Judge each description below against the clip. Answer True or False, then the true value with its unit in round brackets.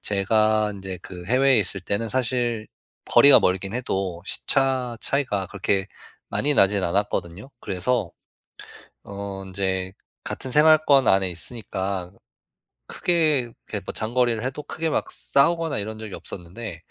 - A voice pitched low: True (110 Hz)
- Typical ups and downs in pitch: True (5.0 semitones)